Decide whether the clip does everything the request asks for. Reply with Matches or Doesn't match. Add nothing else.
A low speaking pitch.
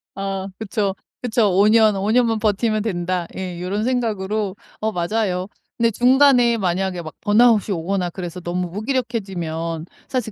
Doesn't match